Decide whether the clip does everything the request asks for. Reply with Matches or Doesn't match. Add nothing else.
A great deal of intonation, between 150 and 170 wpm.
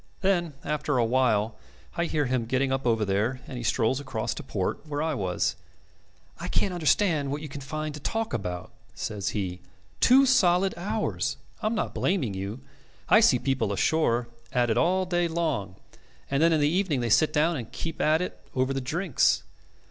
Doesn't match